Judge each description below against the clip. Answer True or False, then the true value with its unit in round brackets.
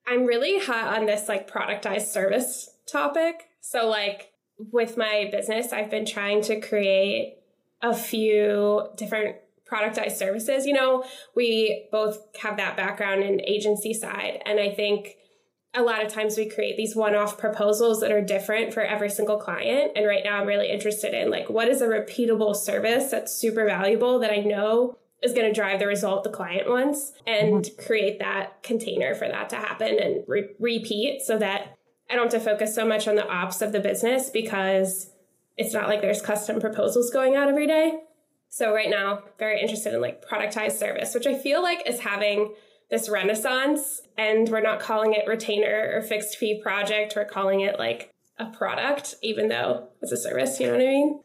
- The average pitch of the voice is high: True (215 Hz)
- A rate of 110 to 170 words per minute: False (190 wpm)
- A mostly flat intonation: True (2.1 semitones)